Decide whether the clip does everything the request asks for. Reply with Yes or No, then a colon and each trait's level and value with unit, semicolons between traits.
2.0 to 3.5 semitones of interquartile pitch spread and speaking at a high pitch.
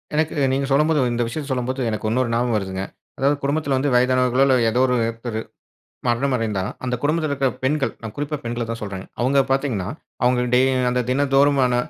No: average, 3.0 semitones; low, 125 Hz